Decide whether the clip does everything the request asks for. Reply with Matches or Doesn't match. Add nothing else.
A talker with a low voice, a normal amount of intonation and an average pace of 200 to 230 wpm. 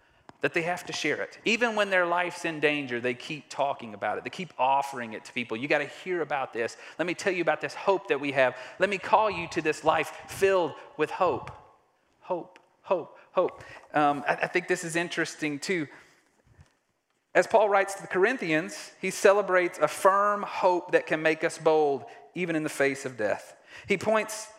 Doesn't match